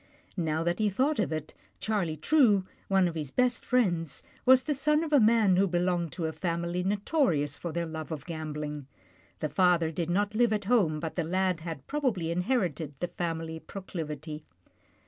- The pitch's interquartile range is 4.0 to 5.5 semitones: Yes, average, 4.7 semitones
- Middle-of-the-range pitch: Yes, medium, 175 Hz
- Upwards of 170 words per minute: Yes, average, 185 wpm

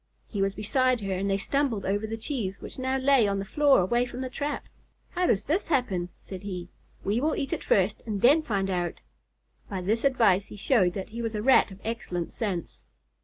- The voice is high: Yes, high, 215 Hz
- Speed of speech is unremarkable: No, fast, 220 wpm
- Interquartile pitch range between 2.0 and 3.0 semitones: No, average, 5.0 semitones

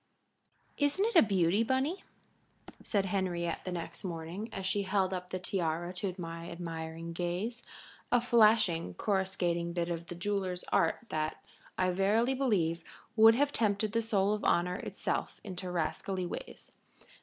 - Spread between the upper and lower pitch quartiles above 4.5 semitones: No, average, 3.8 semitones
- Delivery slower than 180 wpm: Yes, average, 150 wpm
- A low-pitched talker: No, medium, 185 Hz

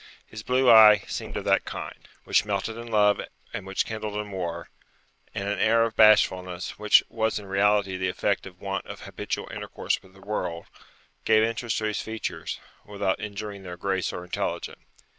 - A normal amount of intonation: No, narrow, 2.2 semitones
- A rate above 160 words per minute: Yes, average, 180 wpm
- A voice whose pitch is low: Yes, low, 105 Hz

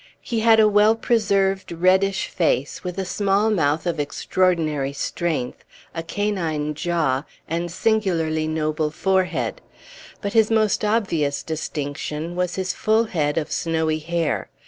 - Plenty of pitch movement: No, average, 4.3 semitones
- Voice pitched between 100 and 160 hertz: No, medium, 175 Hz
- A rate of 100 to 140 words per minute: Yes, slow, 135 wpm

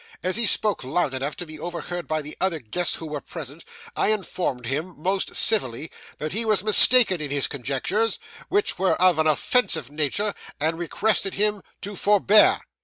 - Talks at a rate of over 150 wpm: Yes, average, 180 wpm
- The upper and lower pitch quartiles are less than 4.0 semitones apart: No, wide, 5.4 semitones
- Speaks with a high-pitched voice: No, medium, 175 Hz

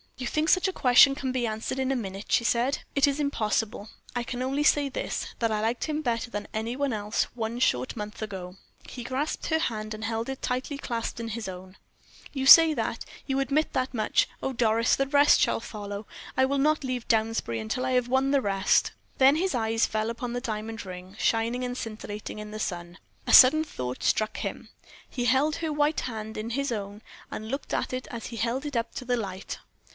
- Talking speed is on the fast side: Yes, fast, 220 wpm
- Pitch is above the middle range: Yes, high, 235 Hz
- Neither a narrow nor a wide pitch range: Yes, average, 3.8 semitones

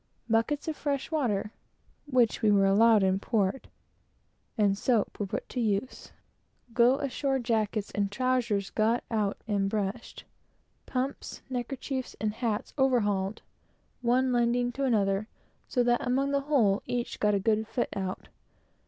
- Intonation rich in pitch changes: No, average, 3.7 semitones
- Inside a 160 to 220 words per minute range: No, average, 145 wpm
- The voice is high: Yes, high, 230 Hz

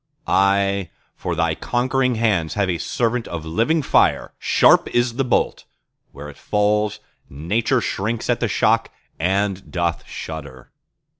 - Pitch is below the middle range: Yes, low, 100 Hz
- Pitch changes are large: Yes, wide, 5.7 semitones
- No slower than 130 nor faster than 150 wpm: Yes, slow, 135 wpm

